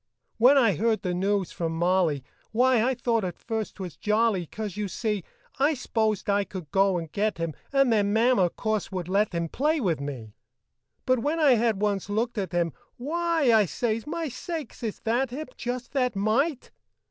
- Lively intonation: No, average, 4.9 semitones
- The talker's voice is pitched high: Yes, high, 215 Hz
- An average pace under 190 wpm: No, average, 195 wpm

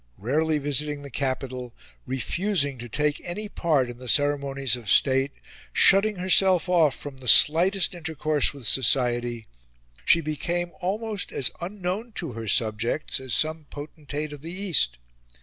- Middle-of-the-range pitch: Yes, medium, 145 Hz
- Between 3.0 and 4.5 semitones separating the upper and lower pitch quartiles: No, average, 4.9 semitones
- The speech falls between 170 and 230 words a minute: No, average, 145 wpm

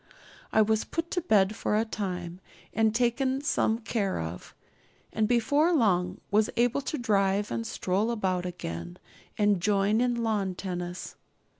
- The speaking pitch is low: No, high, 210 Hz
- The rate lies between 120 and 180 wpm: Yes, average, 150 wpm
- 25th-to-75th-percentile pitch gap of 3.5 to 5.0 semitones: Yes, average, 4.1 semitones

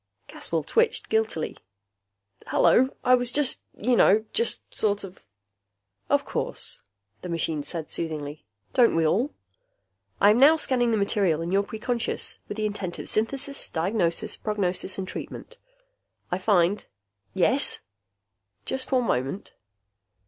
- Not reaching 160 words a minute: Yes, slow, 135 wpm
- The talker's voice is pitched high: Yes, high, 205 Hz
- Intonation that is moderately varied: No, wide, 6.3 semitones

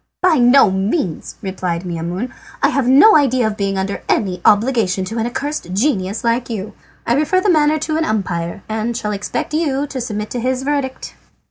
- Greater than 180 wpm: Yes, average, 190 wpm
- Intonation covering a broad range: Yes, wide, 6.0 semitones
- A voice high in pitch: Yes, high, 230 Hz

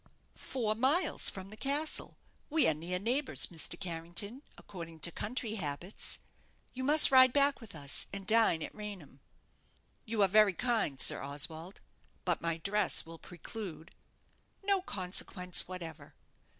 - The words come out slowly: No, average, 145 wpm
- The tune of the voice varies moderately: No, wide, 6.2 semitones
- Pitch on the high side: Yes, high, 195 Hz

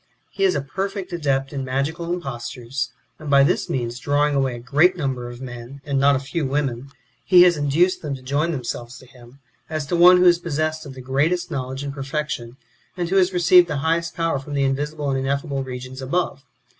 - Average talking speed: No, fast, 210 wpm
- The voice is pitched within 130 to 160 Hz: Yes, medium, 140 Hz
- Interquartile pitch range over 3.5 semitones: Yes, average, 3.9 semitones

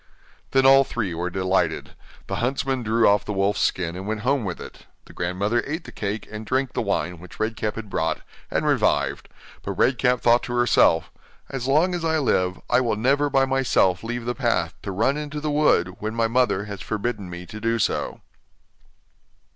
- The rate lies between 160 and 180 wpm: No, average, 200 wpm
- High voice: No, low, 115 Hz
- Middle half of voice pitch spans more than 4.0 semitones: Yes, average, 5.3 semitones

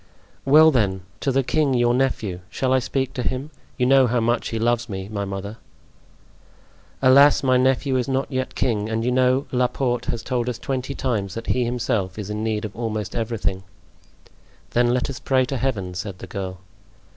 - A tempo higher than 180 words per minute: Yes, average, 190 wpm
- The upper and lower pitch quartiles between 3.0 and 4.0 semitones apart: Yes, average, 3.5 semitones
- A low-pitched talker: Yes, low, 120 Hz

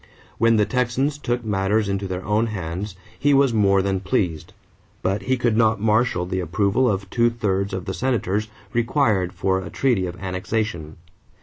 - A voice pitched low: Yes, low, 105 Hz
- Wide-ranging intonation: No, average, 3.8 semitones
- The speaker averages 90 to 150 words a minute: No, average, 175 wpm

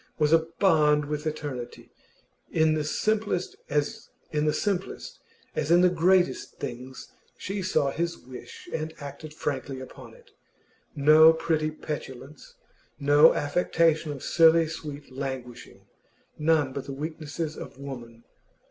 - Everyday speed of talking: No, slow, 120 wpm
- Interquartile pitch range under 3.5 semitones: Yes, average, 2.7 semitones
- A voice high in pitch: No, medium, 155 Hz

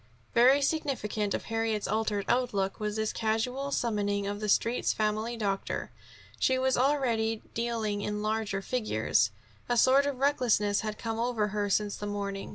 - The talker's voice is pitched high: Yes, high, 220 Hz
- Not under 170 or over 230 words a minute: No, average, 160 wpm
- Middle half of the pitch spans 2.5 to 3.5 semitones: Yes, average, 3.0 semitones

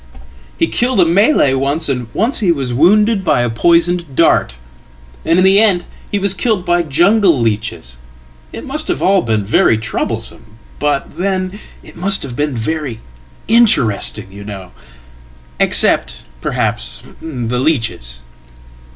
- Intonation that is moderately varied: No, wide, 8.8 semitones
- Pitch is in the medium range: Yes, medium, 150 Hz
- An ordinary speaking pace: No, slow, 130 wpm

